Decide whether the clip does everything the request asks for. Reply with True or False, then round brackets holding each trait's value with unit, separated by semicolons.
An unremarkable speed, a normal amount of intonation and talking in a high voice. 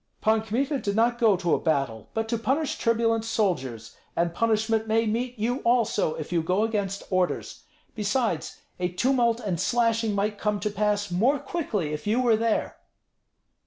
True (170 wpm; 3.6 semitones; 220 Hz)